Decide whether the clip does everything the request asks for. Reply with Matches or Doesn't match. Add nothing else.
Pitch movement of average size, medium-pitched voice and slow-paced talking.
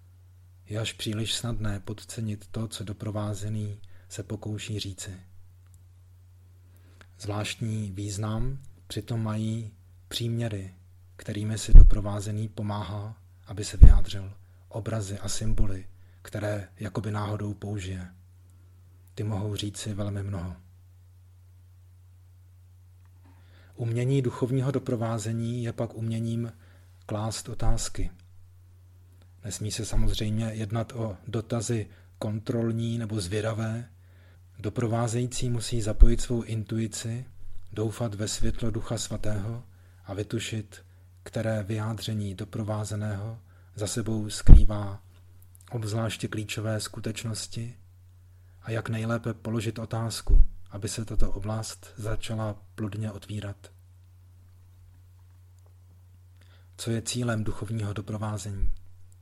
Doesn't match